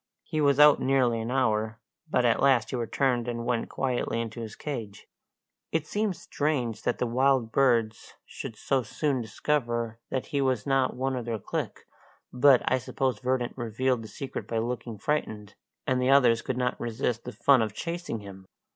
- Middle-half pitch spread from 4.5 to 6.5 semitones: No, average, 3.0 semitones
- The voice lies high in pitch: No, low, 125 Hz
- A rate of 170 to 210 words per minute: Yes, average, 180 wpm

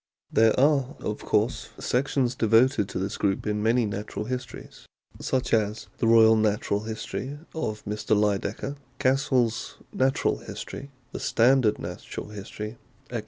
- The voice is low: Yes, low, 115 Hz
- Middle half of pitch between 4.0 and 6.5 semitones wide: No, average, 3.4 semitones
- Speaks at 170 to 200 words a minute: No, slow, 135 wpm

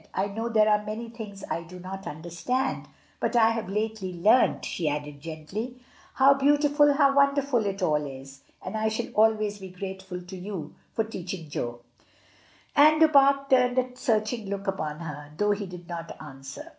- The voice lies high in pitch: Yes, high, 205 Hz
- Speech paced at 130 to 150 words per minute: No, average, 180 wpm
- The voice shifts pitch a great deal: Yes, wide, 5.9 semitones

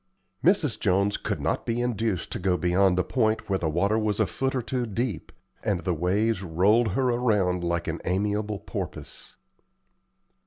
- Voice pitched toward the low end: Yes, low, 105 Hz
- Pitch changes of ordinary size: Yes, average, 4.0 semitones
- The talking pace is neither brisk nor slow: Yes, average, 170 wpm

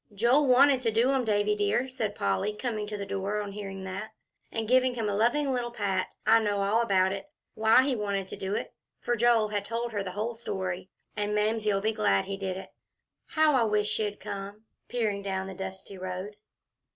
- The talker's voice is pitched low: No, high, 210 Hz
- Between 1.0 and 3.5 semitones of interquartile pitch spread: Yes, average, 2.9 semitones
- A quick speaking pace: Yes, fast, 210 wpm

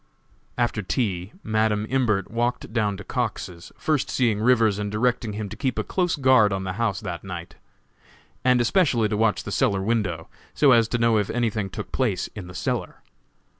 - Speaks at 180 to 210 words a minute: Yes, average, 185 wpm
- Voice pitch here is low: Yes, low, 110 Hz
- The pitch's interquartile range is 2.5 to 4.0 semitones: Yes, average, 3.4 semitones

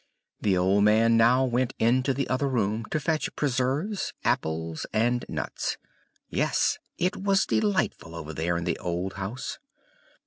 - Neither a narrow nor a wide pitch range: No, wide, 6.0 semitones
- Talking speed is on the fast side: No, average, 145 wpm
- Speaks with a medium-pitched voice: No, low, 115 Hz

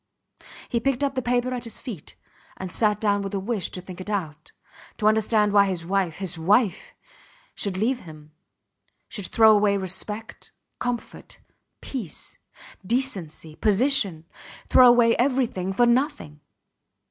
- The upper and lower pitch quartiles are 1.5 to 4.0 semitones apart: No, average, 4.4 semitones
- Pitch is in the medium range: No, high, 210 Hz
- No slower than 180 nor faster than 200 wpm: No, average, 145 wpm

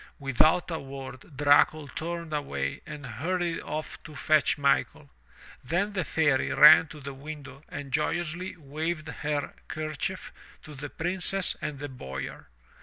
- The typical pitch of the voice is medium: Yes, medium, 150 Hz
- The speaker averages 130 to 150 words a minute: Yes, average, 140 wpm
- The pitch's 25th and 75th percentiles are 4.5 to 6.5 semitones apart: No, average, 2.7 semitones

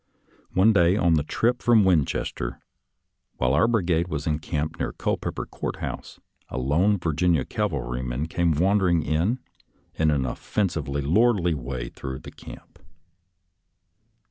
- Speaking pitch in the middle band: No, very low, 80 Hz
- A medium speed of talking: No, slow, 130 wpm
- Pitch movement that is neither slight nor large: Yes, average, 5.0 semitones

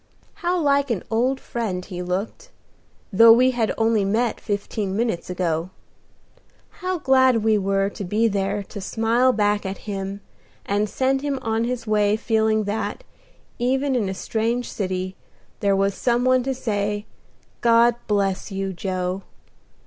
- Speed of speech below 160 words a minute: Yes, average, 150 wpm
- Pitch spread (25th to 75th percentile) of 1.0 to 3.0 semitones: No, average, 3.7 semitones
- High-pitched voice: Yes, high, 215 Hz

